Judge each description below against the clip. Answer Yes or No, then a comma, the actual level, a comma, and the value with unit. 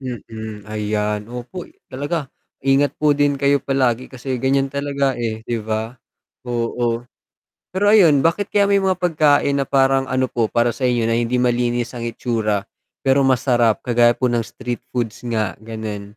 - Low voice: Yes, low, 125 Hz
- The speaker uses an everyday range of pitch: Yes, average, 3.2 semitones